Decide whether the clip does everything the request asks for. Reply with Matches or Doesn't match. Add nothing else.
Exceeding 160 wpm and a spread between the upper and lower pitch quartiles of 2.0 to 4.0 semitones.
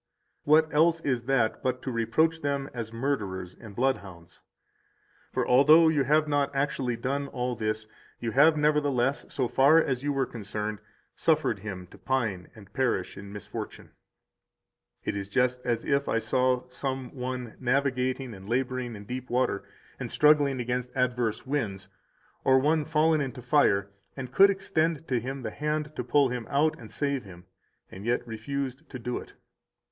Matches